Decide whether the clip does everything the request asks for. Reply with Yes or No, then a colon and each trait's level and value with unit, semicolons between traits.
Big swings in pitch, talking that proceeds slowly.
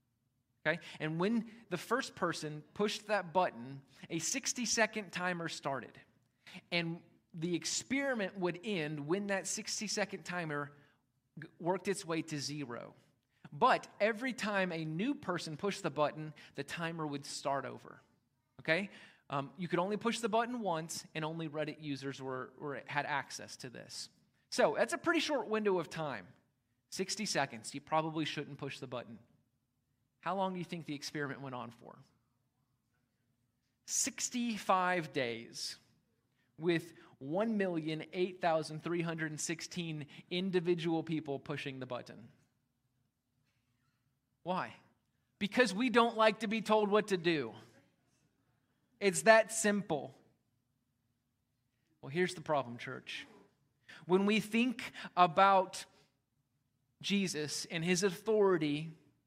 Yes: wide, 6.0 semitones; slow, 125 wpm